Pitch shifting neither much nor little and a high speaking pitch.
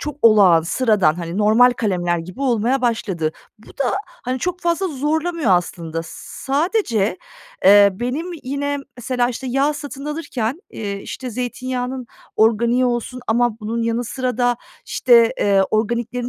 Yes: average, 4.0 semitones; high, 240 Hz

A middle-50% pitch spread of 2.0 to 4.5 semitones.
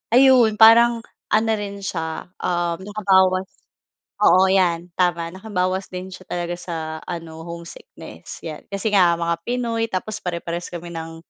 Yes: average, 3.4 semitones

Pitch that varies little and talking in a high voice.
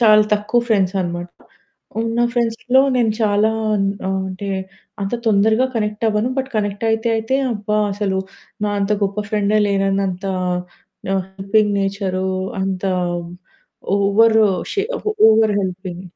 Yes: narrow, 2.3 semitones; high, 210 Hz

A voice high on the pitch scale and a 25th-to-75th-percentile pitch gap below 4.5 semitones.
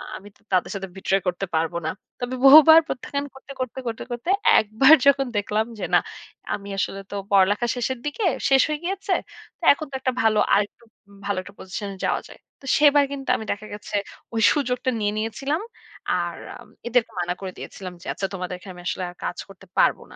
No: high, 220 Hz; wide, 5.6 semitones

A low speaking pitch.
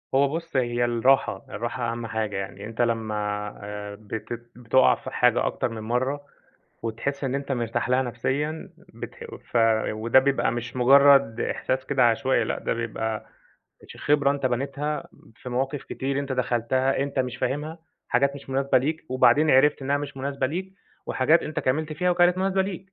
Yes: low, 130 Hz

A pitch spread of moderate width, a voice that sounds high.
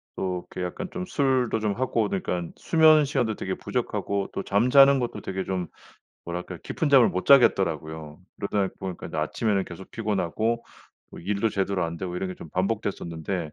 No: average, 4.7 semitones; low, 100 Hz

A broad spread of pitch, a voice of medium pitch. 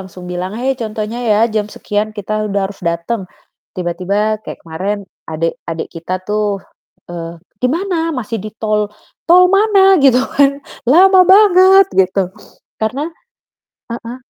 No: wide, 6.6 semitones; high, 215 Hz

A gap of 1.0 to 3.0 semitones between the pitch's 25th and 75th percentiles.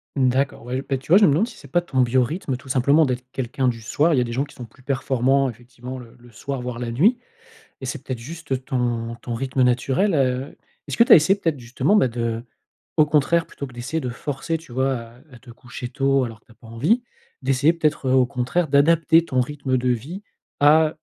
No: average, 3.4 semitones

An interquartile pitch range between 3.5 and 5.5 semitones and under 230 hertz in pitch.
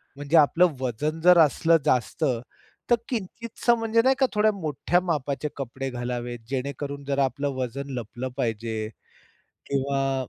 Yes: average, 4.6 semitones; medium, 140 Hz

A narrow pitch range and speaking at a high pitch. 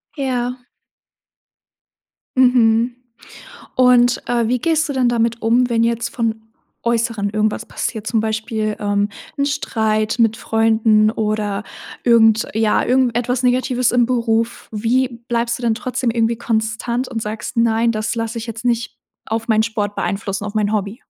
Yes: narrow, 1.8 semitones; high, 230 Hz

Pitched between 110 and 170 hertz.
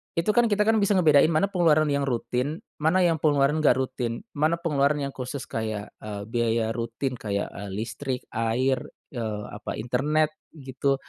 Yes: medium, 140 Hz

